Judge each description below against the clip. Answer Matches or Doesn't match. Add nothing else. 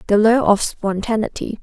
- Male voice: Doesn't match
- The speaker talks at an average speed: Matches